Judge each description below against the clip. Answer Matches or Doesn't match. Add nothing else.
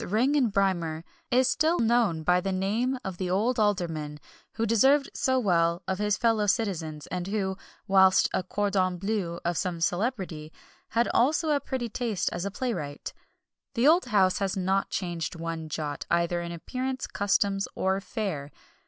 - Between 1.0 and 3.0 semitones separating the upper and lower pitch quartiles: Doesn't match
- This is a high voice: Matches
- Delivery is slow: Doesn't match